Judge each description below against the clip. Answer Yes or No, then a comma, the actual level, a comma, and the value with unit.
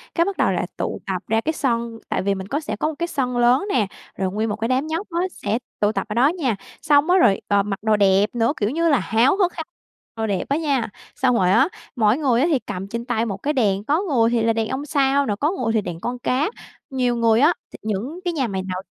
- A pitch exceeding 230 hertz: Yes, high, 240 Hz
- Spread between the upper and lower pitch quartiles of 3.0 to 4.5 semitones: No, average, 5.3 semitones